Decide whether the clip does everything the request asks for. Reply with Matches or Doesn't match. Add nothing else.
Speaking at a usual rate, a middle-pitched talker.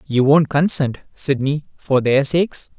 Matches